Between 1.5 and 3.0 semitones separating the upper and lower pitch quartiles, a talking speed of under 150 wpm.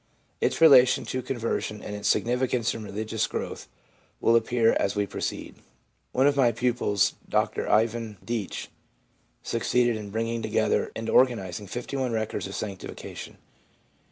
Yes: average, 2.7 semitones; average, 140 wpm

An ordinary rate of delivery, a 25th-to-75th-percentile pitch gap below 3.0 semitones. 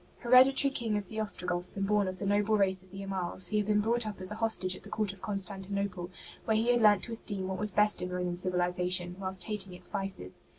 No: fast, 250 wpm; narrow, 2.5 semitones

